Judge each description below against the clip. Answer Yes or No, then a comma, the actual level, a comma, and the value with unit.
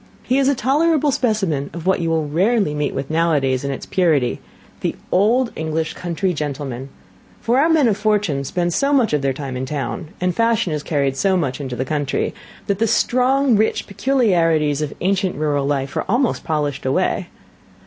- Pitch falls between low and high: Yes, medium, 165 Hz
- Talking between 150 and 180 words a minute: No, average, 190 wpm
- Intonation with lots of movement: Yes, wide, 7.4 semitones